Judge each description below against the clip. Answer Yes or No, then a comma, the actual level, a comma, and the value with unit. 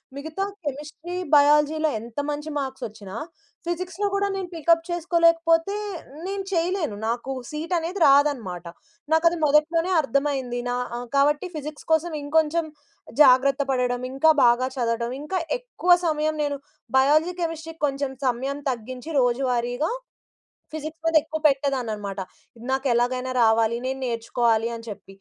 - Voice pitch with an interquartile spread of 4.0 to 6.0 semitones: Yes, average, 4.8 semitones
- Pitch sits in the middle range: No, very high, 285 Hz